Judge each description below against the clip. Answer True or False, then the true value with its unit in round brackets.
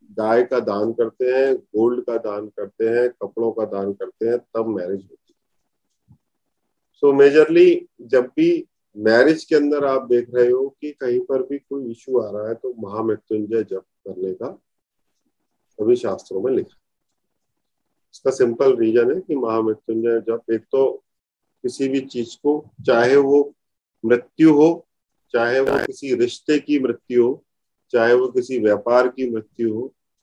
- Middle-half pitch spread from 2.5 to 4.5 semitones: False (5.6 semitones)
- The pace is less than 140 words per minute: False (160 wpm)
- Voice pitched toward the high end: False (125 Hz)